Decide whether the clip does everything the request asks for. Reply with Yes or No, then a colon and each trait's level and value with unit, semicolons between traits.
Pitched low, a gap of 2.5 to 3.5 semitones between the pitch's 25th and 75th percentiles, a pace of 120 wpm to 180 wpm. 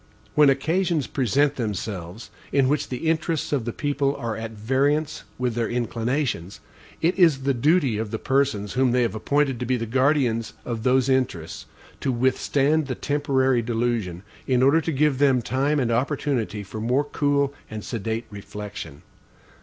No: low, 130 Hz; average, 4.0 semitones; average, 165 wpm